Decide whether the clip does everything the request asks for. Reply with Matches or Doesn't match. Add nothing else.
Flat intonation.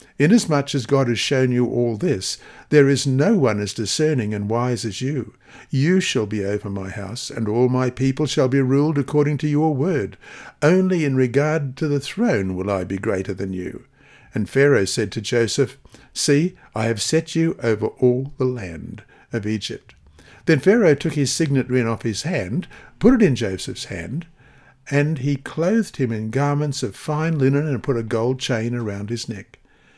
Doesn't match